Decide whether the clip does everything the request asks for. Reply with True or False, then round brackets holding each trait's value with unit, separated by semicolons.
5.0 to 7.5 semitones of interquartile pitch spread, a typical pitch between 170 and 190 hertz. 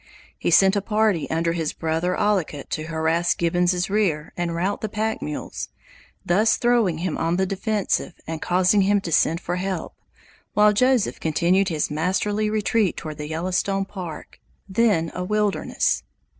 False (3.9 semitones; 185 Hz)